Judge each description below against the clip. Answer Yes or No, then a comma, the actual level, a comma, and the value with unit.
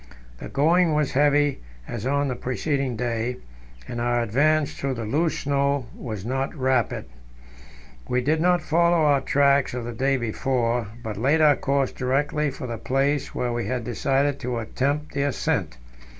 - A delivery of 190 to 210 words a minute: No, average, 165 wpm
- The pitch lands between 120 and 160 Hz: Yes, low, 135 Hz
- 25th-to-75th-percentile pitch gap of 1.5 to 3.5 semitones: Yes, average, 3.1 semitones